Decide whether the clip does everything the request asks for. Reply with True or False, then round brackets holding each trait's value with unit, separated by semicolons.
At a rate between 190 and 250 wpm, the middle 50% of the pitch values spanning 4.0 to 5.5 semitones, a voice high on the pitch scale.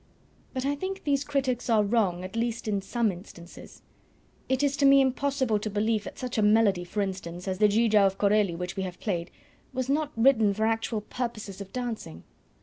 True (200 wpm; 4.6 semitones; 220 Hz)